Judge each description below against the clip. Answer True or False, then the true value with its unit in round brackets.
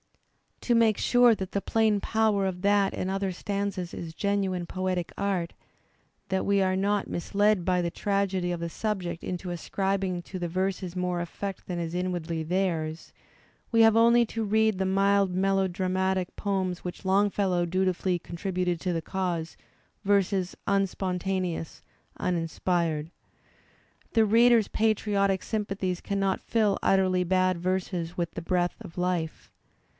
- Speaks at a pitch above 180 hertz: True (190 Hz)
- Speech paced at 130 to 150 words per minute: True (140 wpm)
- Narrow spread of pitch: True (2.1 semitones)